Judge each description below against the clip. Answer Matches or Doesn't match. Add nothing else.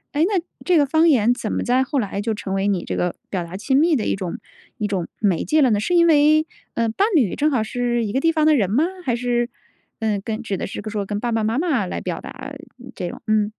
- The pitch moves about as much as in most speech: Doesn't match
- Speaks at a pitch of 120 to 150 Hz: Doesn't match